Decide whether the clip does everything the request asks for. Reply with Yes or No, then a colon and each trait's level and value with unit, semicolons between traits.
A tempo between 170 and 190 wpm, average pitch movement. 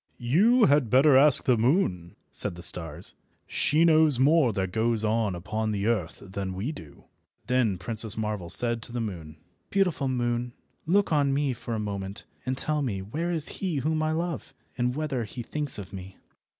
No: average, 185 wpm; wide, 6.8 semitones